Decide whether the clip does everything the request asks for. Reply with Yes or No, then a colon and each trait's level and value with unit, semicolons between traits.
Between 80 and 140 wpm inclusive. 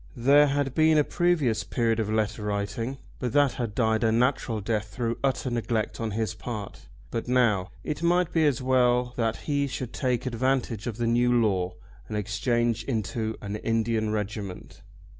No: average, 175 wpm